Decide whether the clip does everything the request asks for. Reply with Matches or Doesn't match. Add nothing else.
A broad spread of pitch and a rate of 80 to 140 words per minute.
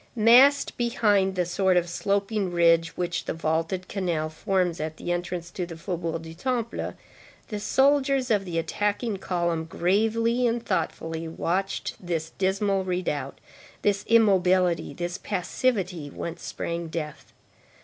Doesn't match